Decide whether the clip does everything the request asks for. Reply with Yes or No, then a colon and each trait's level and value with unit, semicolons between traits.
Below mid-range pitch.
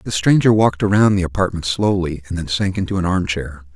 Yes: very low, 90 Hz